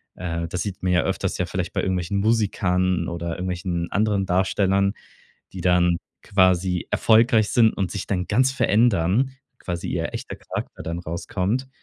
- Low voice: Yes, very low, 95 Hz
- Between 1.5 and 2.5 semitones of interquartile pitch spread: No, average, 2.9 semitones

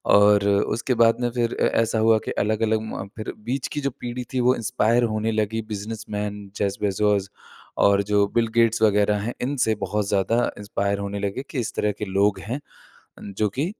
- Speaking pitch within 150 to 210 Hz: No, low, 110 Hz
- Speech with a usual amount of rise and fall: No, narrow, 2.3 semitones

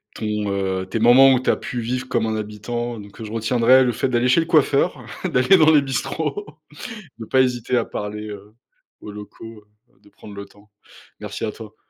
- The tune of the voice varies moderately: Yes, average, 3.5 semitones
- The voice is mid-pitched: No, low, 115 Hz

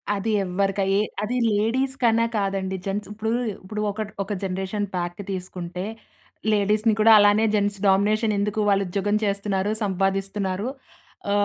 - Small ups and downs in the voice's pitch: Yes, narrow, 1.7 semitones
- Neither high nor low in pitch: No, high, 200 Hz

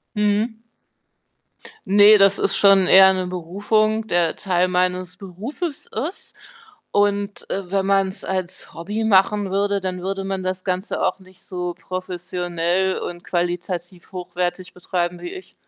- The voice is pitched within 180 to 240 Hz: Yes, high, 190 Hz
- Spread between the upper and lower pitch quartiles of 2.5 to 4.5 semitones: No, narrow, 2.1 semitones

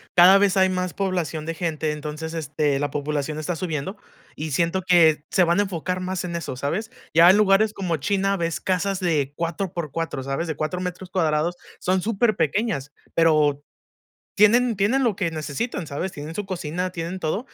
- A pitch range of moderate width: Yes, average, 3.7 semitones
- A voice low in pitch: No, medium, 170 Hz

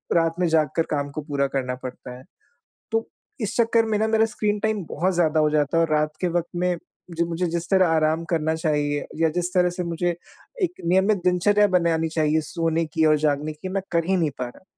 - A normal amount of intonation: Yes, average, 3.1 semitones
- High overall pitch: No, medium, 165 Hz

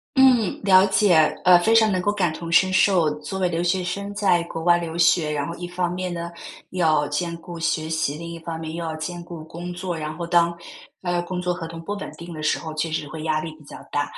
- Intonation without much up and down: Yes, narrow, 2.0 semitones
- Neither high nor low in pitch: Yes, medium, 170 Hz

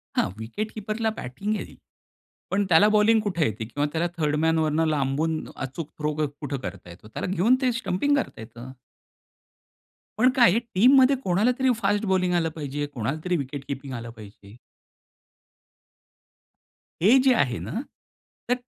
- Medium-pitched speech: Yes, medium, 160 Hz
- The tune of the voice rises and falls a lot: Yes, wide, 7.8 semitones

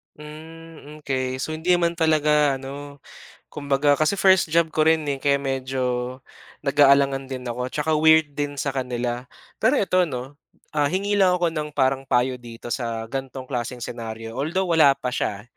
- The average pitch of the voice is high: No, medium, 140 Hz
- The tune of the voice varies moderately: Yes, average, 3.6 semitones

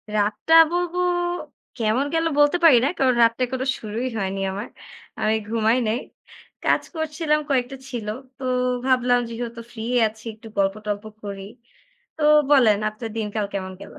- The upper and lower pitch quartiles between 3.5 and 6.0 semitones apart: Yes, average, 3.9 semitones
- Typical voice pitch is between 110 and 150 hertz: No, high, 230 Hz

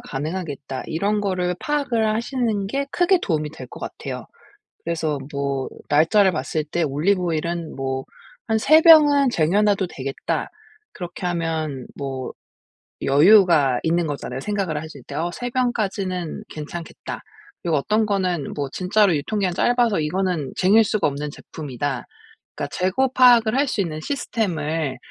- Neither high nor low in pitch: Yes, medium, 175 Hz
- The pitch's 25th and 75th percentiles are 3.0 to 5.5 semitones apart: No, wide, 6.1 semitones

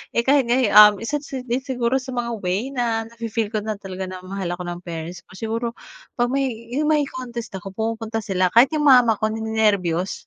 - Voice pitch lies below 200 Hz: No, high, 225 Hz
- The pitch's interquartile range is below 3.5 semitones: No, average, 4.2 semitones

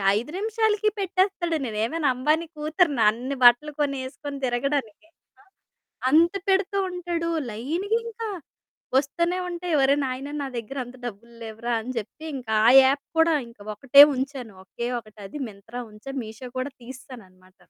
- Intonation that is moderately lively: No, wide, 5.9 semitones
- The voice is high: Yes, very high, 275 Hz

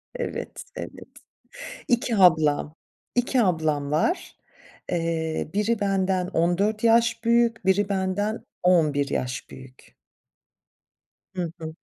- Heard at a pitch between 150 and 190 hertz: Yes, medium, 185 Hz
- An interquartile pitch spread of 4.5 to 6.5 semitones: Yes, wide, 5.5 semitones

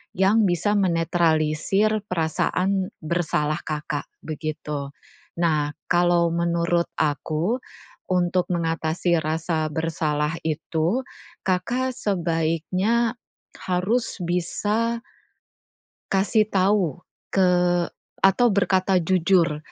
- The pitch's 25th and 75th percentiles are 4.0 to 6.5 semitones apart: No, average, 3.3 semitones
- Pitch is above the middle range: No, medium, 175 Hz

